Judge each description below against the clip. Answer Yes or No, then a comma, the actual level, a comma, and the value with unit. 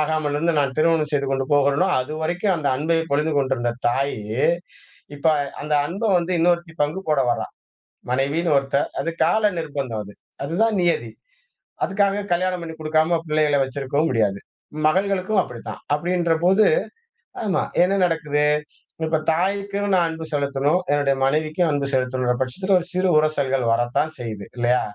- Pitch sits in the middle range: Yes, medium, 155 Hz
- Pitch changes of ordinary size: Yes, average, 4.1 semitones